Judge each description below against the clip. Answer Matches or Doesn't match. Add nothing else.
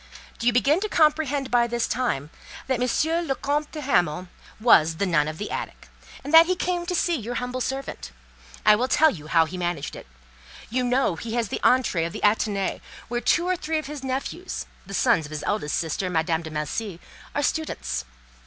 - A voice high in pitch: Matches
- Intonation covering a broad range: Matches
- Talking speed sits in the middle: Doesn't match